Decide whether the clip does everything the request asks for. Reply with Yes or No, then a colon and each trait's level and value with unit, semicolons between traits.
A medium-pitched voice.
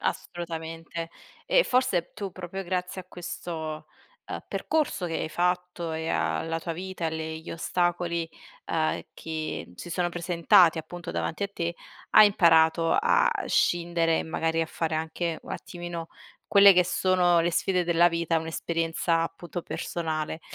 Yes: medium, 170 Hz